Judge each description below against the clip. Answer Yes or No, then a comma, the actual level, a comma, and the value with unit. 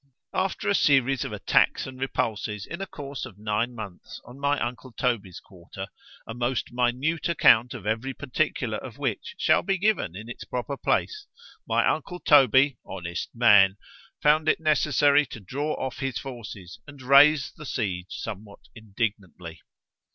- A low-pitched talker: Yes, low, 125 Hz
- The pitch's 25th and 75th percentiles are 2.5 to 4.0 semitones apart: No, average, 5.2 semitones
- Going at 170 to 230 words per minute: No, average, 160 wpm